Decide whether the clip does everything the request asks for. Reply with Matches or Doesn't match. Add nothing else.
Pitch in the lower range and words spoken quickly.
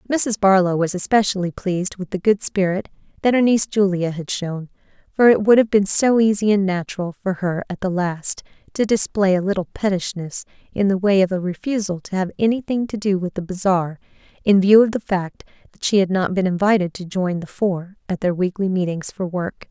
Doesn't match